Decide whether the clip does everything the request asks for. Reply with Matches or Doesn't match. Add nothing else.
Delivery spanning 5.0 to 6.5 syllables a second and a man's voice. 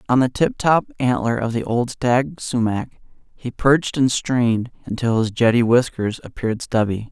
Doesn't match